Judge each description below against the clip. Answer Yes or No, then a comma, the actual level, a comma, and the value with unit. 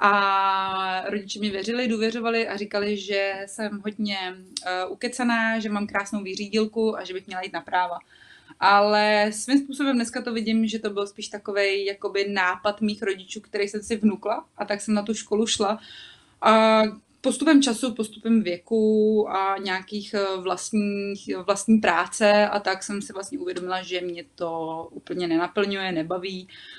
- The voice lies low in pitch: No, high, 205 Hz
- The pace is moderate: Yes, average, 155 wpm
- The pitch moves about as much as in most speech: No, narrow, 2.2 semitones